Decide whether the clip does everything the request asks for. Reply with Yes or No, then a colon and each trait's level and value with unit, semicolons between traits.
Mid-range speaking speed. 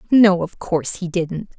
Yes: average, 190 wpm